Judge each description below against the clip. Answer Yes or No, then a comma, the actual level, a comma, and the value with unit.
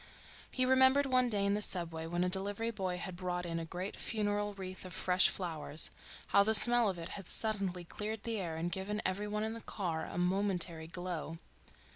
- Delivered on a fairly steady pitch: No, average, 3.1 semitones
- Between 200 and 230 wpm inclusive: Yes, fast, 205 wpm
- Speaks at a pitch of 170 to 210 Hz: Yes, high, 190 Hz